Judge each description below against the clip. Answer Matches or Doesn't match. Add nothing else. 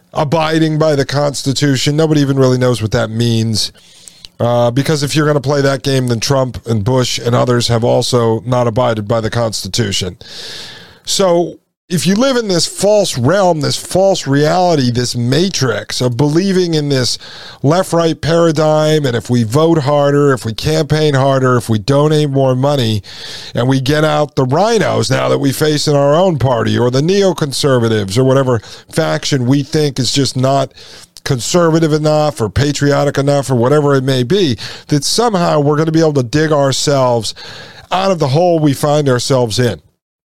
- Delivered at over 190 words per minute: Doesn't match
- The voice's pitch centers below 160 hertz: Matches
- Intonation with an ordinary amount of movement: Matches